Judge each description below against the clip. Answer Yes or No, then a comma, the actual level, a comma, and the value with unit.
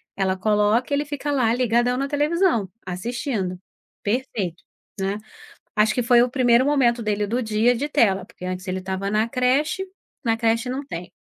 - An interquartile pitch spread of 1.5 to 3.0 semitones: No, average, 4.2 semitones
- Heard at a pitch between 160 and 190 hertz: No, high, 235 Hz